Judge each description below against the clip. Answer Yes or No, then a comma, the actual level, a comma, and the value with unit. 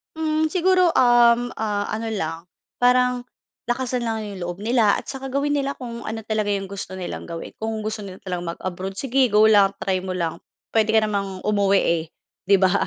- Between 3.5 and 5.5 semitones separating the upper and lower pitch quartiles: Yes, average, 4.0 semitones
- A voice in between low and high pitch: No, high, 215 Hz